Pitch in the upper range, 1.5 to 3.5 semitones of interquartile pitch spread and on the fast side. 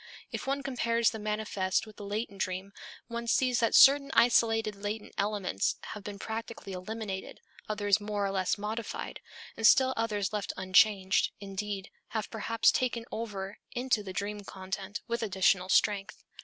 No: high, 210 Hz; narrow, 2.6 semitones; average, 155 wpm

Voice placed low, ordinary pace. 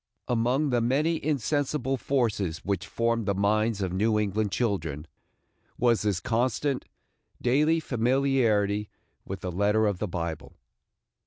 No: low, 110 Hz; slow, 130 wpm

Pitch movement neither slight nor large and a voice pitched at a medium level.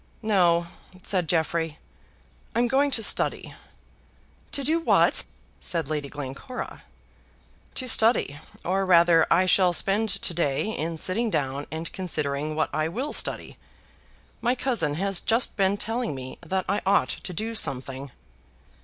No: wide, 6.1 semitones; medium, 180 Hz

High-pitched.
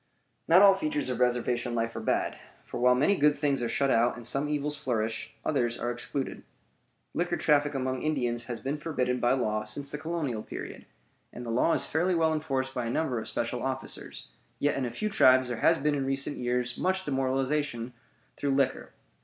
No: low, 135 Hz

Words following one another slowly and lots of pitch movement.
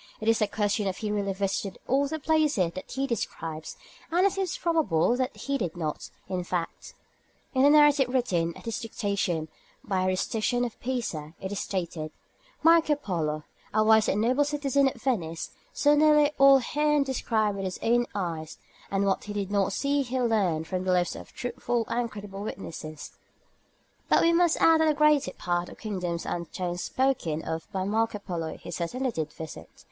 No: average, 190 wpm; wide, 7.1 semitones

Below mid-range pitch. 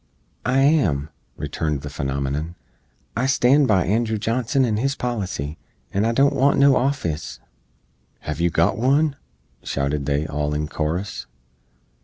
Yes: low, 100 Hz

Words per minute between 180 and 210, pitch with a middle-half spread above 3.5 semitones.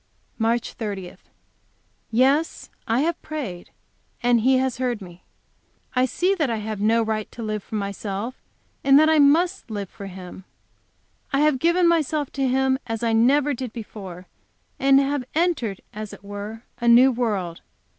No: average, 165 wpm; average, 4.7 semitones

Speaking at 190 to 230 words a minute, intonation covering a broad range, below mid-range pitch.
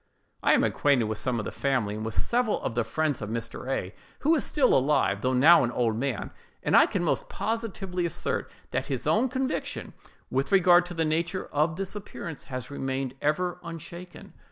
No: average, 200 wpm; wide, 6.0 semitones; medium, 150 Hz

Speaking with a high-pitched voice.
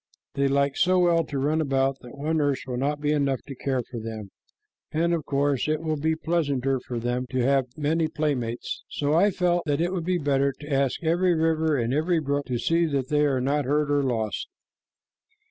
No: medium, 145 Hz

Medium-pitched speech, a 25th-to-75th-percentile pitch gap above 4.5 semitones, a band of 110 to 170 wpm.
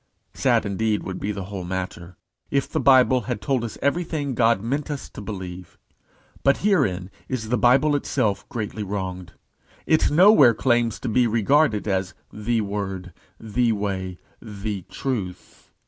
No: low, 110 Hz; average, 5.1 semitones; average, 155 wpm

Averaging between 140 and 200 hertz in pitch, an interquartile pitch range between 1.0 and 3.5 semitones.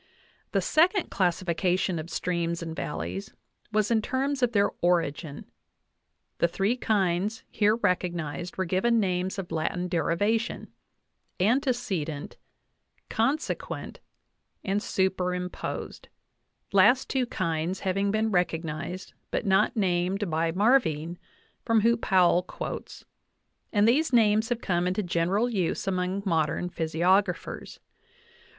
No: medium, 185 Hz; average, 4.0 semitones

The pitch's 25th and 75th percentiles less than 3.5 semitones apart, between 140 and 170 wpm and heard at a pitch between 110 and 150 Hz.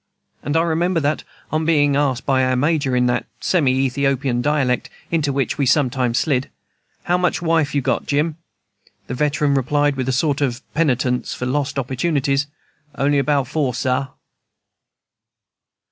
Yes: narrow, 2.6 semitones; average, 155 wpm; medium, 140 Hz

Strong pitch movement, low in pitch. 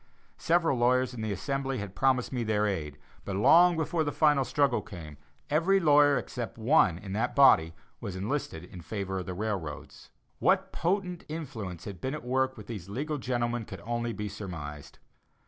Yes: wide, 6.8 semitones; low, 120 Hz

